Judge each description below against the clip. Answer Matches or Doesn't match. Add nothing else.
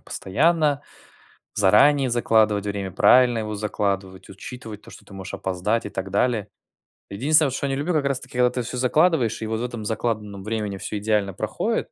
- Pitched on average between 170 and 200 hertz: Doesn't match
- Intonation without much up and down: Doesn't match